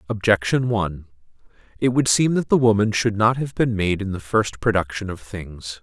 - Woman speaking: No, male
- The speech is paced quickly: No, average, 195 wpm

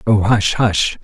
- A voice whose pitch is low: Yes, low, 105 Hz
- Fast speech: No, average, 175 wpm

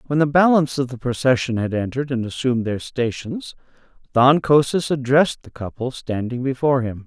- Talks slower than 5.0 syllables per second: No, 5.8 syllables/s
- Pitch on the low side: Yes, low, 130 Hz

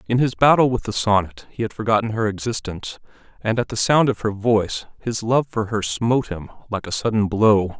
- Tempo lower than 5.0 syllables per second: No, 5.6 syllables/s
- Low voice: Yes, low, 110 Hz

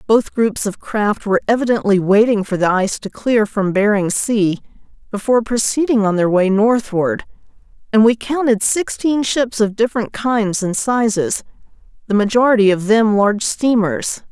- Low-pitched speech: No, high, 215 Hz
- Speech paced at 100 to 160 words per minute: Yes, average, 155 wpm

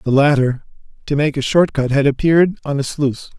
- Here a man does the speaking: Yes, male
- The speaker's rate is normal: No, fast, 215 wpm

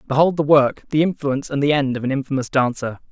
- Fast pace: Yes, fast, 230 wpm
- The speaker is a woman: No, male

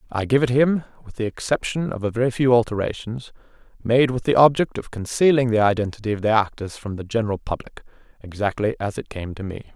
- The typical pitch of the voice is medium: No, low, 115 Hz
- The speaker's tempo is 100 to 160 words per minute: No, fast, 205 wpm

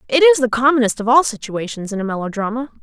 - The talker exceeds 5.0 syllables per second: Yes, 6.7 syllables/s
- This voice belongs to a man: No, female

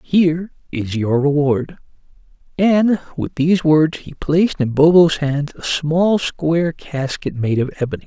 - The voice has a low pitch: No, medium, 155 Hz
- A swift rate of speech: No, average, 150 wpm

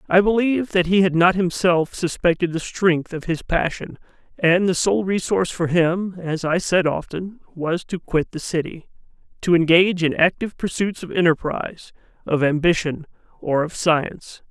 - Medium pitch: Yes, medium, 175 Hz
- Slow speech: No, average, 160 wpm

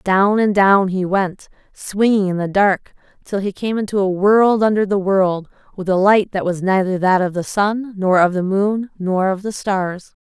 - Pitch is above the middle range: Yes, high, 195 Hz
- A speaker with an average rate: No, fast, 210 wpm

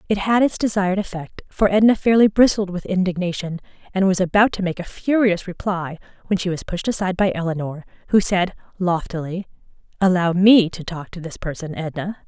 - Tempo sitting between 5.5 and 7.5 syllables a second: Yes, 5.7 syllables/s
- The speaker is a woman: Yes, female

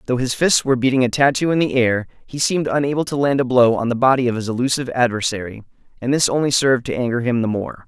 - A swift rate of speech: Yes, fast, 250 wpm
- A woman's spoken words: No, male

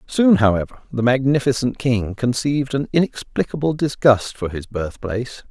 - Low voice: Yes, low, 125 Hz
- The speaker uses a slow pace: Yes, slow, 130 wpm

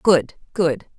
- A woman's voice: Yes, female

